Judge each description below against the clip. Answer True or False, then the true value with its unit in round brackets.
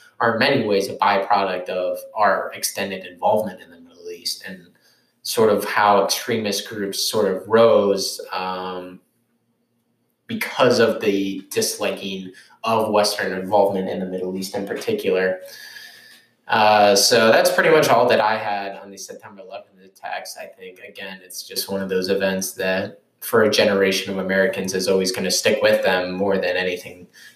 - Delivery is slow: False (165 wpm)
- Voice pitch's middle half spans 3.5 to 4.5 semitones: True (3.8 semitones)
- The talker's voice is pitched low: True (100 Hz)